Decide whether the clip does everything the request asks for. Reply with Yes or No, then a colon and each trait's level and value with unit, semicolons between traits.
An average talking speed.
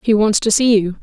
No: fast, 295 wpm